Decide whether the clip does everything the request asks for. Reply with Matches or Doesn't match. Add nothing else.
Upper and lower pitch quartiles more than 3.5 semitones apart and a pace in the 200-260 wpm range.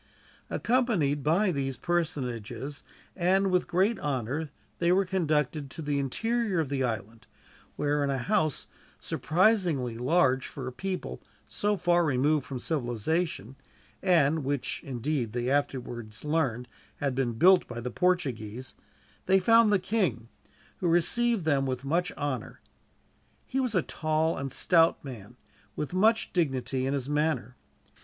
Doesn't match